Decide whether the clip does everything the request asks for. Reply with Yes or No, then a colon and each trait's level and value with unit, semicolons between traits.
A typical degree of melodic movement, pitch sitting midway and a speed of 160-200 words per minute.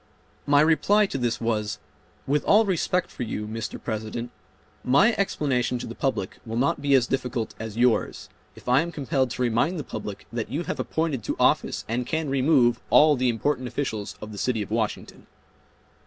No: average, 4.5 semitones; low, 125 Hz; average, 185 wpm